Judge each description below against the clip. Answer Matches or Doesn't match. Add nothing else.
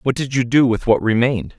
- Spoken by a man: Matches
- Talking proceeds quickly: Matches